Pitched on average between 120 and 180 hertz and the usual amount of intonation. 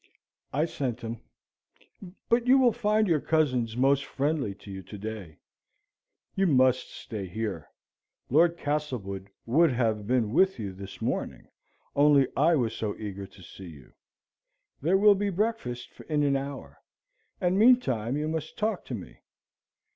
No: low, 135 Hz; wide, 7.4 semitones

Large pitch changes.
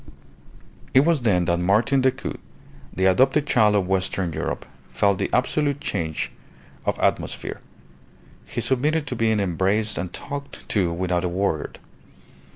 Yes: wide, 6.4 semitones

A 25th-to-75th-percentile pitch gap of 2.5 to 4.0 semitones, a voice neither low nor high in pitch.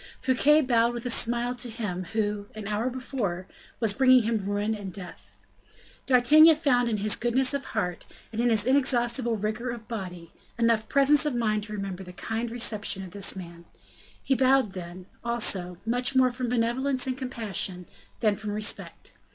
No: average, 3.7 semitones; high, 230 Hz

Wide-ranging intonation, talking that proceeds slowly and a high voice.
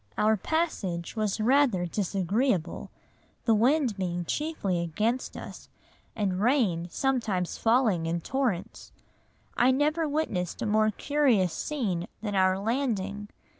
Yes: wide, 6.0 semitones; slow, 120 wpm; high, 215 Hz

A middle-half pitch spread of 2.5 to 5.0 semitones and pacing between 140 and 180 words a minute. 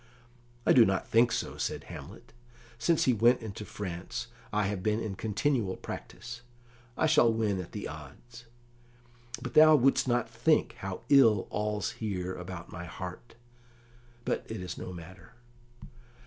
Yes: average, 4.4 semitones; average, 150 wpm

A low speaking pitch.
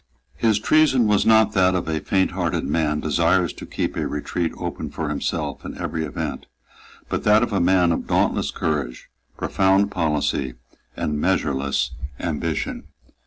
Yes: very low, 85 Hz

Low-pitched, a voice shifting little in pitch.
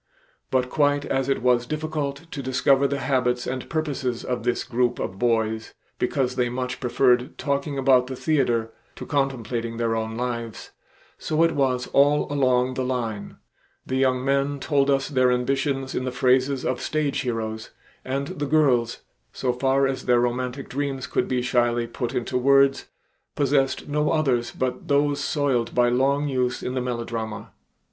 Yes: low, 130 Hz; narrow, 2.2 semitones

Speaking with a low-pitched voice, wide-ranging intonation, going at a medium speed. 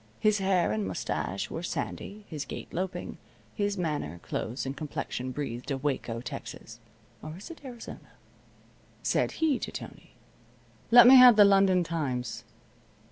No: medium, 165 Hz; wide, 8.2 semitones; average, 145 wpm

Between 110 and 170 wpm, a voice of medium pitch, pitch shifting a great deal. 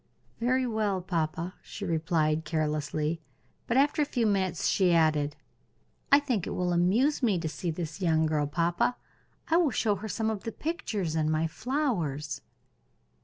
Yes: average, 165 wpm; medium, 180 Hz; wide, 6.2 semitones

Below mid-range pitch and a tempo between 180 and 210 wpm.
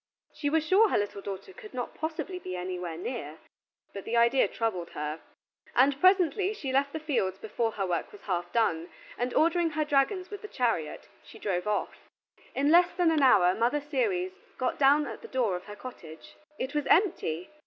No: very high, 255 Hz; average, 195 wpm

